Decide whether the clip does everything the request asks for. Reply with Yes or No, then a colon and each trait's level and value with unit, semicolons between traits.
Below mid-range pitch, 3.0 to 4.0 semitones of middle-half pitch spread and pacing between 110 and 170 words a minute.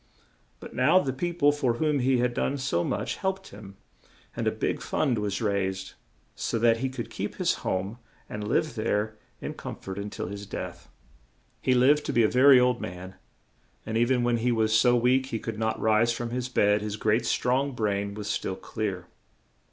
No: low, 115 Hz; average, 3.6 semitones; fast, 205 wpm